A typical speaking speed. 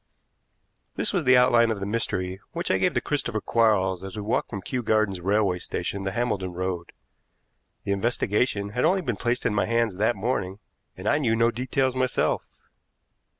Yes: average, 185 wpm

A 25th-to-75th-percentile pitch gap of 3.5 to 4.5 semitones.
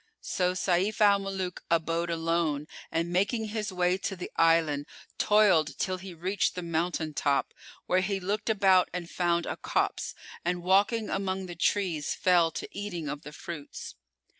No: average, 2.7 semitones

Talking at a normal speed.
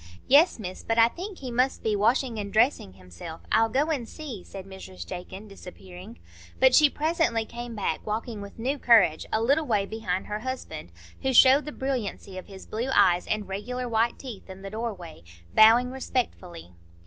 Yes: average, 185 wpm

